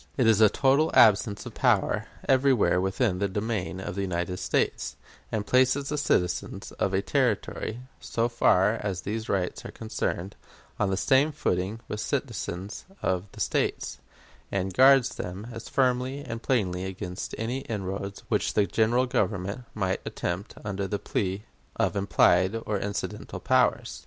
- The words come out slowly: No, average, 155 wpm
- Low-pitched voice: Yes, low, 105 Hz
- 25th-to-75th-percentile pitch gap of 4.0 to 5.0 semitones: Yes, average, 4.4 semitones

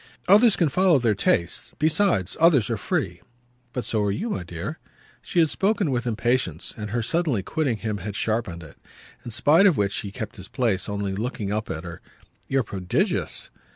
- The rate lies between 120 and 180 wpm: No, average, 190 wpm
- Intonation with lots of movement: Yes, wide, 7.8 semitones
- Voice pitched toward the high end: No, low, 115 Hz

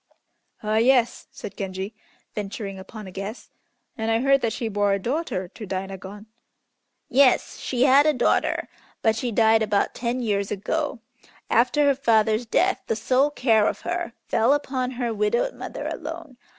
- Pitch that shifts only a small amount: No, average, 3.8 semitones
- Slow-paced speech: No, average, 165 wpm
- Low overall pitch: No, high, 225 Hz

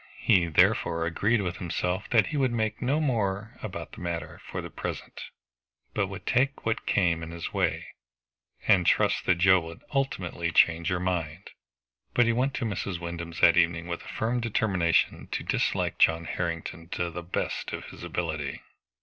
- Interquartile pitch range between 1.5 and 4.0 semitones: No, average, 4.5 semitones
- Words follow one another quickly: No, average, 175 wpm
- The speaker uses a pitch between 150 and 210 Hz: No, very low, 90 Hz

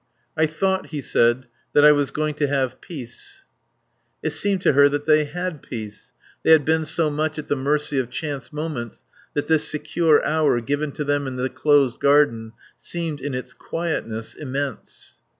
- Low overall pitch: No, medium, 145 Hz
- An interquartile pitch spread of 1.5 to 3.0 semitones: Yes, average, 2.7 semitones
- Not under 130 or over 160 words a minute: No, average, 180 wpm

